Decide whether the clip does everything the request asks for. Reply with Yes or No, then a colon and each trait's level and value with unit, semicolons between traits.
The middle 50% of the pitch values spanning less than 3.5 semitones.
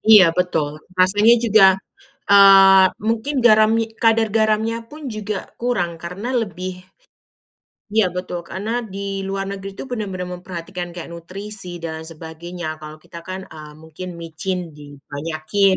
No: average, 3.8 semitones